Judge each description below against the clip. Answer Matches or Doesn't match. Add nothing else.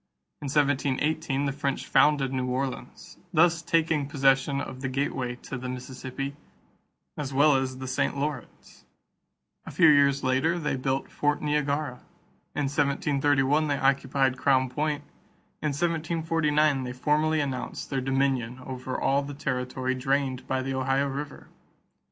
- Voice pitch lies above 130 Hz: Matches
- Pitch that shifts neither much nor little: Doesn't match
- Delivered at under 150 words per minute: Matches